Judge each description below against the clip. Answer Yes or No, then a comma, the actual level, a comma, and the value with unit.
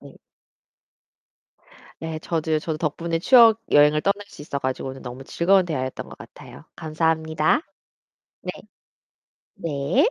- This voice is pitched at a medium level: Yes, medium, 160 Hz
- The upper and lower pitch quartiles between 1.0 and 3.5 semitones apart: Yes, narrow, 2.6 semitones